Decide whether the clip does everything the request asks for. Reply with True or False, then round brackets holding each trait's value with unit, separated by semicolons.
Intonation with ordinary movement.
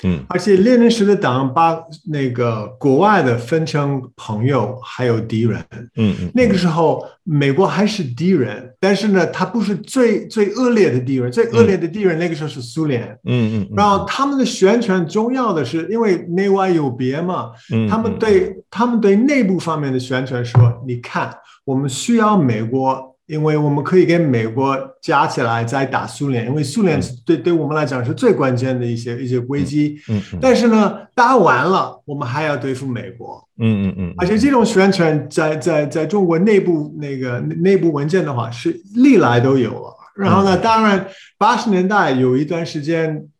False (7.2 semitones)